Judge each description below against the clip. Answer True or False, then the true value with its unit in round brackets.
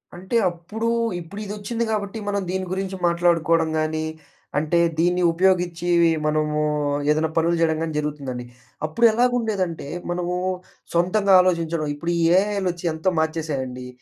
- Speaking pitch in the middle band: True (170 Hz)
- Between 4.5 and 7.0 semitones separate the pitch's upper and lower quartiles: False (3.3 semitones)